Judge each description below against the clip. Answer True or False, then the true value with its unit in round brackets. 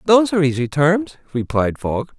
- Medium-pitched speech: True (155 Hz)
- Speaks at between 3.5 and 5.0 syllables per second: False (5.5 syllables/s)